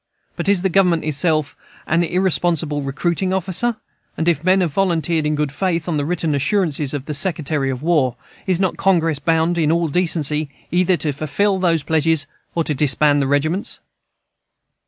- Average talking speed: Yes, average, 175 wpm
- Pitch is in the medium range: Yes, medium, 165 Hz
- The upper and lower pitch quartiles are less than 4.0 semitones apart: Yes, average, 3.2 semitones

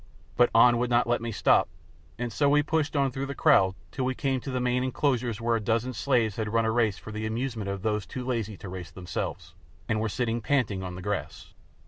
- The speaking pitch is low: Yes, low, 115 Hz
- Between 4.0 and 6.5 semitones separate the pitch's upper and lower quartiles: No, average, 3.2 semitones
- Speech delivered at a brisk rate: Yes, fast, 235 wpm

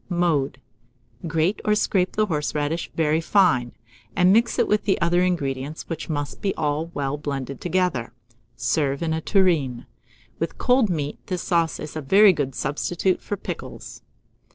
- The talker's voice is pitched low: No, medium, 160 Hz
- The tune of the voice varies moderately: Yes, average, 4.1 semitones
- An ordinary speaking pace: Yes, average, 155 wpm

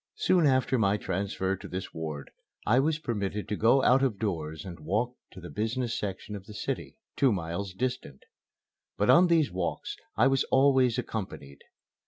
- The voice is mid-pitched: No, low, 105 Hz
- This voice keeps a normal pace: Yes, average, 175 wpm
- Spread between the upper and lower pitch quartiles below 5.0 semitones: No, wide, 5.6 semitones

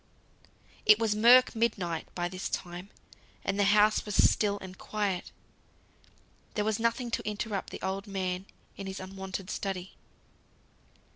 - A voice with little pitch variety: Yes, narrow, 2.1 semitones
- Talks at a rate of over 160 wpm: No, average, 140 wpm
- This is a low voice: No, high, 195 Hz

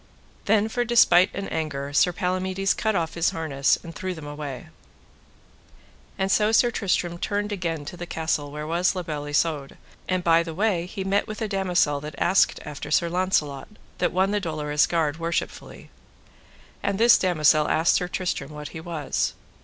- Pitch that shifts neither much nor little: Yes, average, 4.0 semitones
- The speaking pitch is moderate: Yes, medium, 170 Hz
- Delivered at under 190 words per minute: Yes, average, 175 wpm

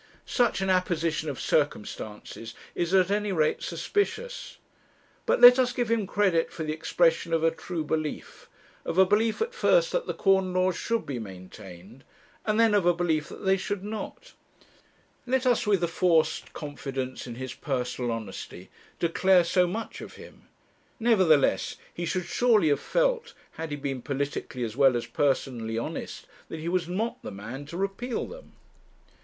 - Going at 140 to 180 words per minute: Yes, average, 170 wpm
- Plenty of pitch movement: Yes, wide, 6.7 semitones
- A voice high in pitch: No, medium, 170 Hz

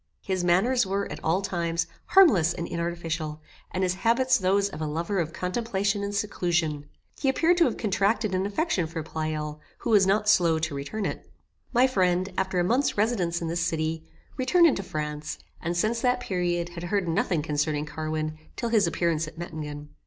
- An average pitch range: Yes, average, 4.5 semitones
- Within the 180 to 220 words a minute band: Yes, average, 185 wpm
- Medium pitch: Yes, medium, 180 Hz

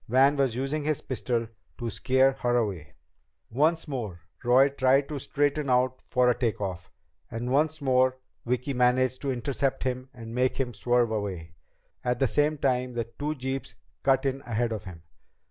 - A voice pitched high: No, low, 130 Hz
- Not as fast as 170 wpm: No, average, 175 wpm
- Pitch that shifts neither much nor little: No, narrow, 2.3 semitones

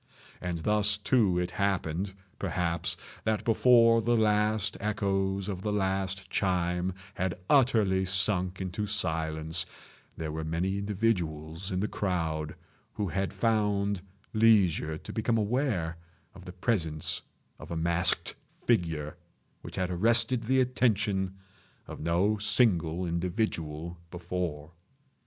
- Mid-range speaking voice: No, very low, 95 Hz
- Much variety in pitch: No, average, 3.7 semitones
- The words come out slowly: Yes, slow, 120 wpm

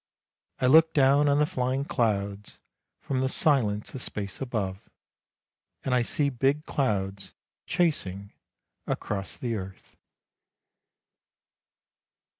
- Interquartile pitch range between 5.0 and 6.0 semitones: Yes, wide, 5.6 semitones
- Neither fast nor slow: No, slow, 105 wpm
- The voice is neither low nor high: No, low, 125 Hz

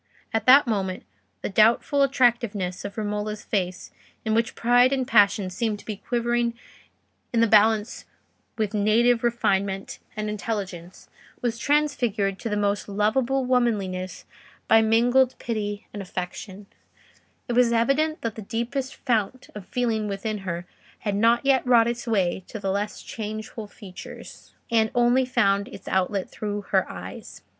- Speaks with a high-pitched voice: Yes, high, 220 Hz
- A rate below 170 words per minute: Yes, average, 150 wpm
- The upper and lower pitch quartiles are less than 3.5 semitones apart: Yes, average, 3.0 semitones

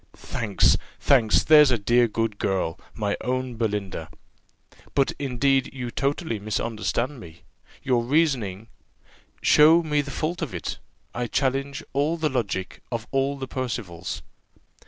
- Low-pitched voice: Yes, low, 125 Hz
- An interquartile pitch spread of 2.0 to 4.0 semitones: No, average, 4.5 semitones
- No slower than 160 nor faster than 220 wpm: No, slow, 135 wpm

